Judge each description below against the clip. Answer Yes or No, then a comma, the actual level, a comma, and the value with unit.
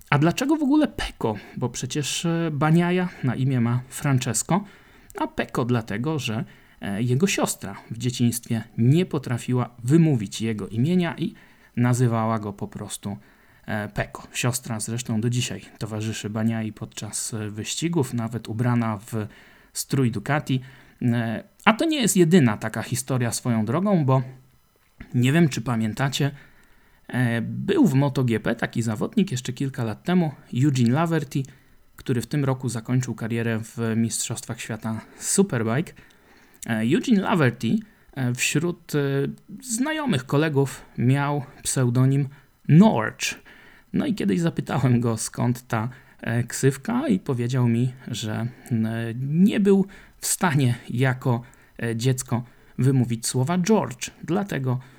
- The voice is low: Yes, low, 125 Hz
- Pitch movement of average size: Yes, average, 4.6 semitones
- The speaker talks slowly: No, average, 120 wpm